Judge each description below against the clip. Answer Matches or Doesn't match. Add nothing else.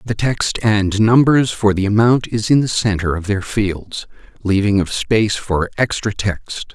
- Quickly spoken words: Doesn't match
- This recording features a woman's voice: Doesn't match